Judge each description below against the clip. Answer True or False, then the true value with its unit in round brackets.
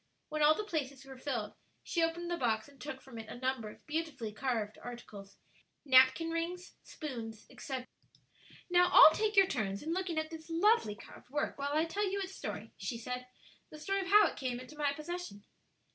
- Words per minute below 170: False (200 wpm)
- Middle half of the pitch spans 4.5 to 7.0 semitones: True (5.4 semitones)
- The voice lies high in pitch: True (295 Hz)